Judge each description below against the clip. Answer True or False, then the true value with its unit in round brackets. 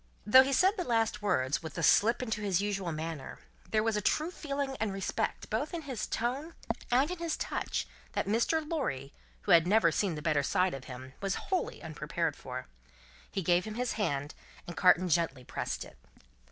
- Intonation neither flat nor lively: False (7.7 semitones)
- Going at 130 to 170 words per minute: False (195 wpm)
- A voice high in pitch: True (205 Hz)